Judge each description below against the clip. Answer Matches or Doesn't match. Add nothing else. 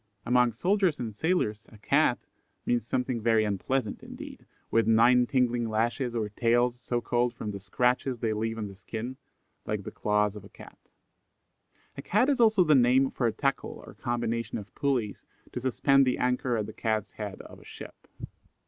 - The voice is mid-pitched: Doesn't match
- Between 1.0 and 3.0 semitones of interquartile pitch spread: Matches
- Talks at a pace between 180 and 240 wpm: Matches